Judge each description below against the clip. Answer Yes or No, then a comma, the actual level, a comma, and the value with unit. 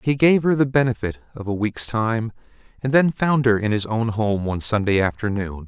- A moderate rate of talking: No, fast, 210 wpm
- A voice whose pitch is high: No, low, 115 Hz